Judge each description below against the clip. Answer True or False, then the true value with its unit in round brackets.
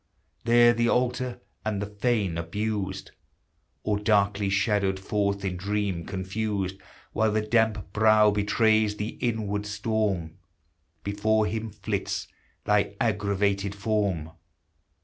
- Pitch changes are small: True (1.7 semitones)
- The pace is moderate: False (110 wpm)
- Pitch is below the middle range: True (105 Hz)